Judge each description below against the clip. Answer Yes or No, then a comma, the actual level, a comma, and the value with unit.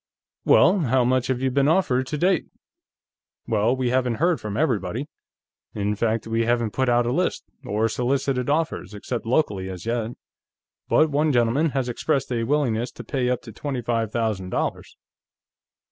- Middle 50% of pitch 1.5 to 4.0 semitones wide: Yes, average, 3.4 semitones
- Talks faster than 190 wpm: No, average, 170 wpm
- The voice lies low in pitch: Yes, low, 125 Hz